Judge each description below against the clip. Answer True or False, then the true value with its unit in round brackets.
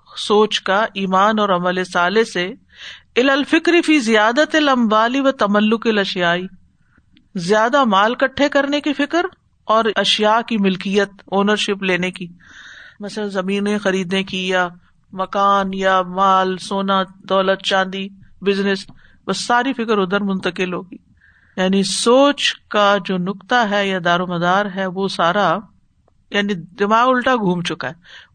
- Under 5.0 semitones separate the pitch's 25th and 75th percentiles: True (3.1 semitones)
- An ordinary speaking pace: True (125 wpm)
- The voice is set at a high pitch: True (200 Hz)